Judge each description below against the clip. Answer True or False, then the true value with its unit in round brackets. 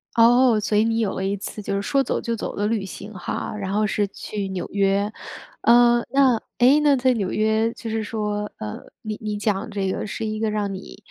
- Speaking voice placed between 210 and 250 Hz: True (215 Hz)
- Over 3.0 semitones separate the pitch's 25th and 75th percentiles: False (2.4 semitones)